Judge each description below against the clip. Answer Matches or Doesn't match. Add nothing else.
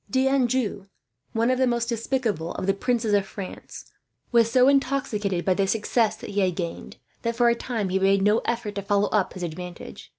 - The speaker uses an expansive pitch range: Doesn't match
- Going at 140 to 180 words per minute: Doesn't match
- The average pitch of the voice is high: Matches